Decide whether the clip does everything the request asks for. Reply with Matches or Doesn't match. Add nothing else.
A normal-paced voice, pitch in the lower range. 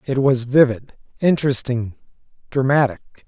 Doesn't match